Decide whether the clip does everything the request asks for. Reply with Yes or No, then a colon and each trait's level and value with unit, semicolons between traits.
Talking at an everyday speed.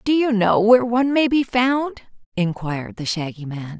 Yes: average, 190 wpm